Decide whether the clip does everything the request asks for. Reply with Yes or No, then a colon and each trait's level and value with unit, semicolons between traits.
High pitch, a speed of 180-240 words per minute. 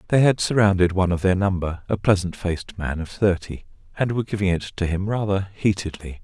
No: very low, 95 Hz; average, 200 wpm